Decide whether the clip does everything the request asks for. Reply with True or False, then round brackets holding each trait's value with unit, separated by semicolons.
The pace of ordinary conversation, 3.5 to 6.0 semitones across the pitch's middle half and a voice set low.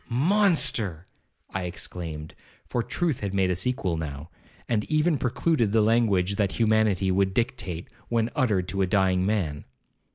True (150 wpm; 4.7 semitones; 100 Hz)